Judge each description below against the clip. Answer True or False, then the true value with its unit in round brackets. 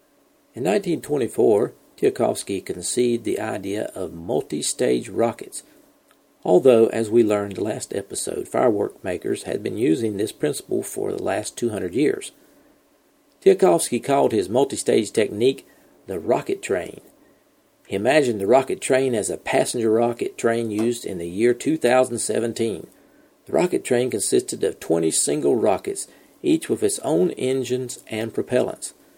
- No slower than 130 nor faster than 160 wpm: True (135 wpm)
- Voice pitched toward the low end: True (120 Hz)